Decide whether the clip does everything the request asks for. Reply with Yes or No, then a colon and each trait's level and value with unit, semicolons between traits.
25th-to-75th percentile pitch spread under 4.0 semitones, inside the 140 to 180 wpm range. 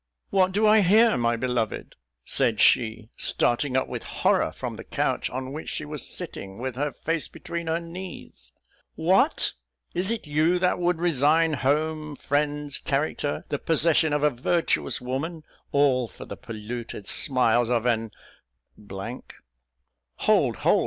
No: average, 5.2 semitones; average, 150 wpm